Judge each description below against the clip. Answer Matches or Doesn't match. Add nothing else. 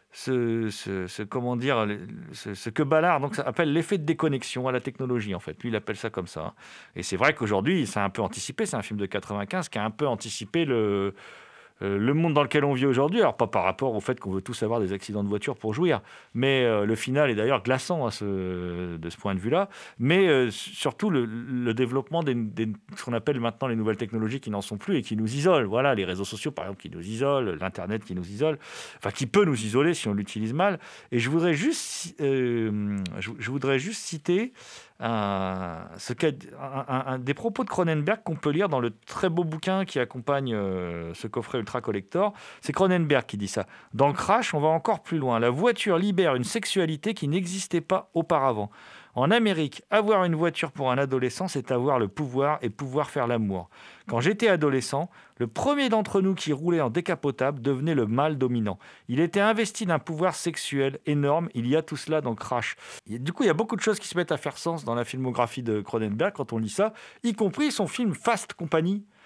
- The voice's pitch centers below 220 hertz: Matches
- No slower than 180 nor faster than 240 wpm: Matches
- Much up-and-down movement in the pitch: Matches